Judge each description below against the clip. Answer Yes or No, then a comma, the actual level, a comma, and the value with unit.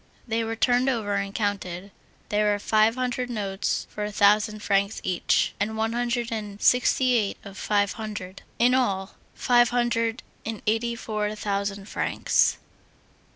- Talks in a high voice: Yes, high, 215 Hz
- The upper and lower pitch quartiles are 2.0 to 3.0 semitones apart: Yes, average, 2.7 semitones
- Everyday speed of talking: Yes, average, 155 wpm